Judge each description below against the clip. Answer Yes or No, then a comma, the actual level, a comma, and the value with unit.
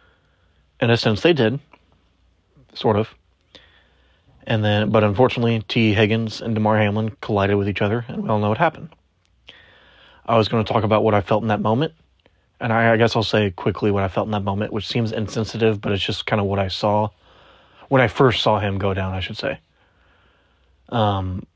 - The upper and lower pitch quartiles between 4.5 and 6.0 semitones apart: No, average, 2.8 semitones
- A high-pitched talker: No, low, 105 Hz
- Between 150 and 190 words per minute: No, average, 200 wpm